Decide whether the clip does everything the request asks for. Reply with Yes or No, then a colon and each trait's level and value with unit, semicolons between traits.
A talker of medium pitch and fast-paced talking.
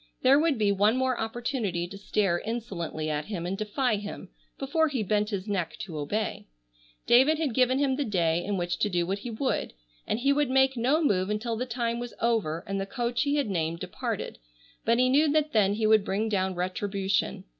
No: high, 215 Hz; fast, 210 wpm